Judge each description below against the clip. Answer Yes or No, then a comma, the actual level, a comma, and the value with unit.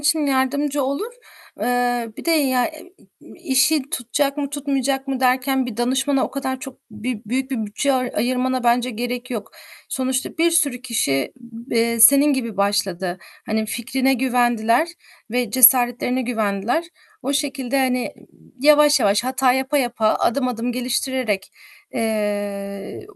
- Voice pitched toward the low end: No, very high, 255 Hz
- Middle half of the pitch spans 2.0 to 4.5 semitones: Yes, average, 2.7 semitones